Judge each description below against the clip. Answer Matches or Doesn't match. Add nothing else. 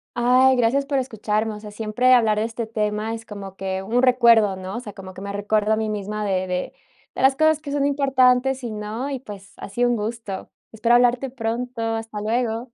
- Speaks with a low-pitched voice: Doesn't match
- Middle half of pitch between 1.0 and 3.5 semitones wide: Matches